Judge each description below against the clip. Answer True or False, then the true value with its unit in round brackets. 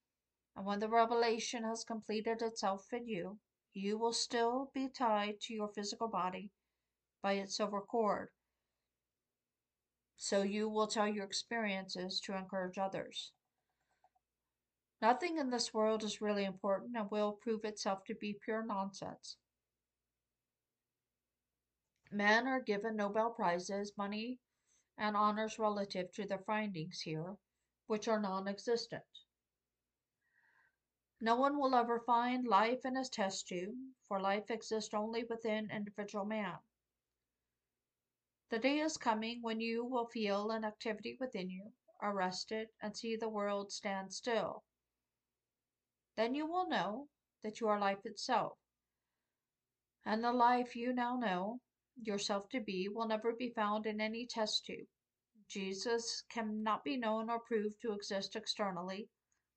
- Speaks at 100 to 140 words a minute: True (135 wpm)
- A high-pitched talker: True (210 Hz)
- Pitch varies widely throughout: False (3.0 semitones)